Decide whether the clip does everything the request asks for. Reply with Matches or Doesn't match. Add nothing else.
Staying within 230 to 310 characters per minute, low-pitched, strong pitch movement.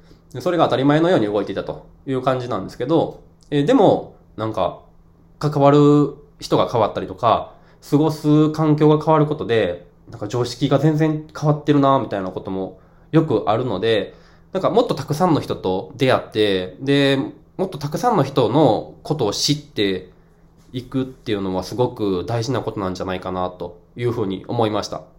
Doesn't match